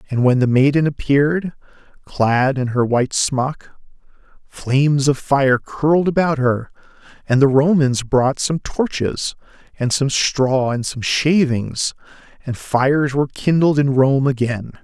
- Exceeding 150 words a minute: No, average, 140 wpm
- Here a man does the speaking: Yes, male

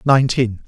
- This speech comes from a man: Yes, male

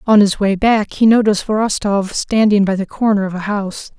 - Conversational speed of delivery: No, fast, 210 wpm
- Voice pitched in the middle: No, high, 205 Hz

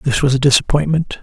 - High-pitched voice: No, medium, 140 Hz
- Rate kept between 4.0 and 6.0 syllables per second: No, 6.4 syllables/s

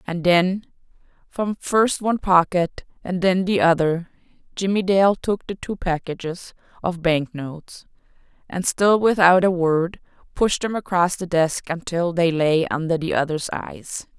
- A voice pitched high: No, medium, 180 Hz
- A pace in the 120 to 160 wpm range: Yes, average, 150 wpm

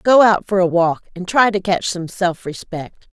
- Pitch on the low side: No, medium, 185 Hz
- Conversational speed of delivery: No, fast, 230 wpm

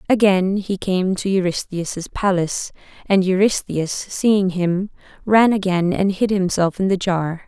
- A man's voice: No, female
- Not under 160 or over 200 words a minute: No, average, 145 wpm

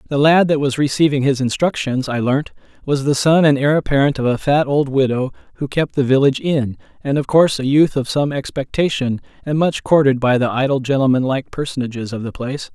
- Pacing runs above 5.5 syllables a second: Yes, 5.7 syllables/s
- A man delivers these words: Yes, male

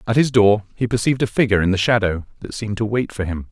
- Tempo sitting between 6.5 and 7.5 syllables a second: Yes, 7.1 syllables/s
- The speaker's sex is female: No, male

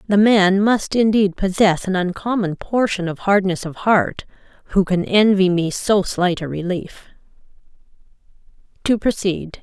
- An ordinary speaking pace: No, slow, 130 wpm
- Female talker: Yes, female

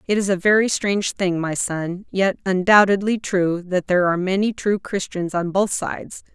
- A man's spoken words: No, female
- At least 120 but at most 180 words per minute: No, average, 190 wpm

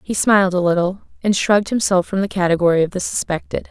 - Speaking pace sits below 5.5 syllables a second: No, 6.5 syllables/s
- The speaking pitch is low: No, medium, 185 Hz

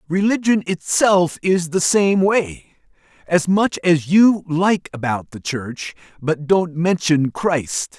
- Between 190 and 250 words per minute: No, slow, 135 wpm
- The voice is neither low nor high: Yes, medium, 175 Hz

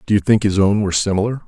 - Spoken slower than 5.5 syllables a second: No, 7.6 syllables/s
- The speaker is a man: Yes, male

